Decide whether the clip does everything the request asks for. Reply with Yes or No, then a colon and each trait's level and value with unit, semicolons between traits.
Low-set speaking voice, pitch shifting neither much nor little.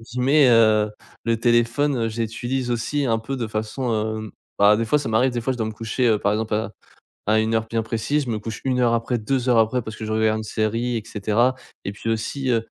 No: low, 115 Hz; narrow, 2.2 semitones